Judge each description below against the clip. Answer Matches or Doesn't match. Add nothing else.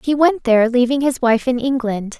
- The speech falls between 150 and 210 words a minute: Doesn't match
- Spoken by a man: Doesn't match